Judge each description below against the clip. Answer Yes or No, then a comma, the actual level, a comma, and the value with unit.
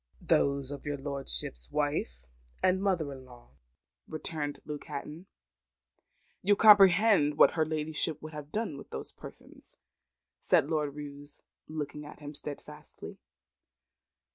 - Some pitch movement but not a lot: No, narrow, 1.9 semitones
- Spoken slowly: Yes, slow, 125 wpm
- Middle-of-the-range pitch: Yes, medium, 150 Hz